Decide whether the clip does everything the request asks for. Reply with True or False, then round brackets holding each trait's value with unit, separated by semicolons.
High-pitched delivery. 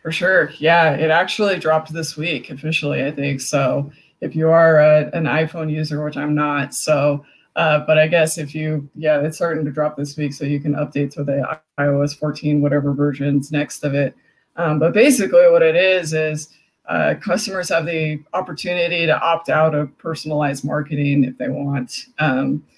False (150 Hz)